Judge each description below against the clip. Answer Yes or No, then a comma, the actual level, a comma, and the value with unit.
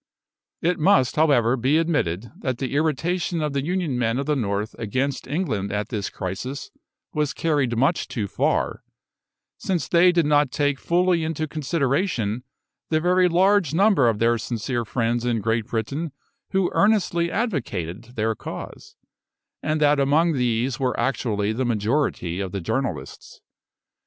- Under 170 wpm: Yes, average, 150 wpm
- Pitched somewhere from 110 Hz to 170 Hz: Yes, low, 135 Hz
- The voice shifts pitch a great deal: Yes, wide, 6.1 semitones